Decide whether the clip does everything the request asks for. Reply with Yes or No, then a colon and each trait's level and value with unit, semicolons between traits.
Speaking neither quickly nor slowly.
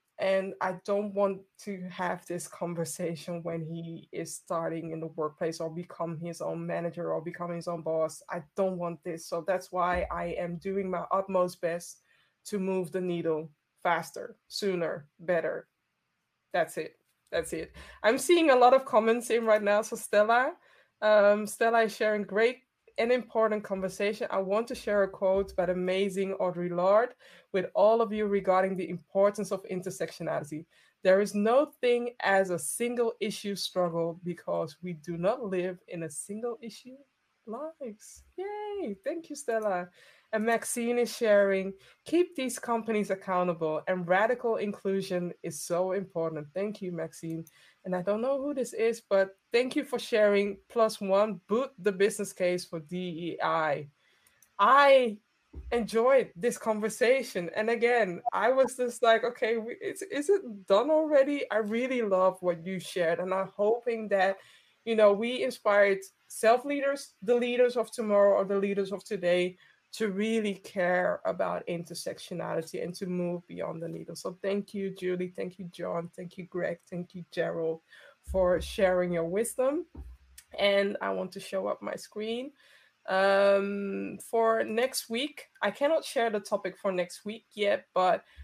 Yes: average, 160 wpm